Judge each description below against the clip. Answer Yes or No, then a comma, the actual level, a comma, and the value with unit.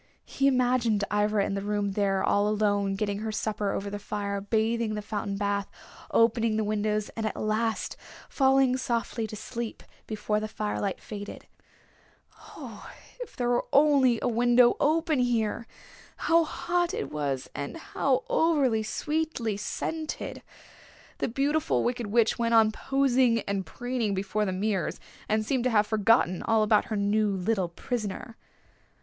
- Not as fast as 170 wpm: Yes, average, 155 wpm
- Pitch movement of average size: Yes, average, 3.3 semitones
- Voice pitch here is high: Yes, high, 220 Hz